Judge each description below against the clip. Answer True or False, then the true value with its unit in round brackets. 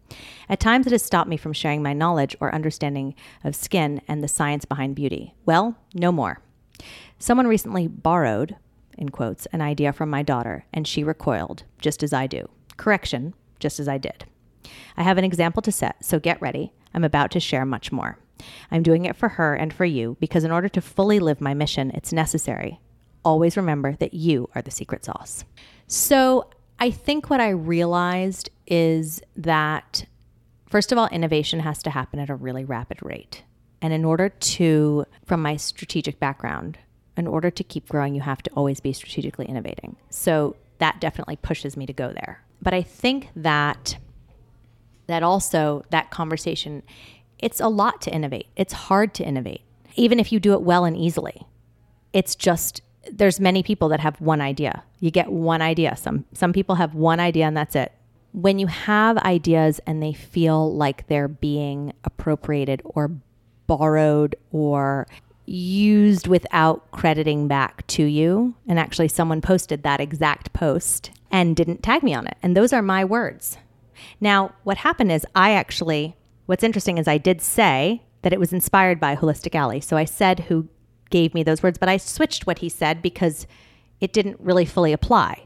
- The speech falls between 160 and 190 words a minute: True (180 wpm)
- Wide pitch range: False (4.2 semitones)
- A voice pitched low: False (160 Hz)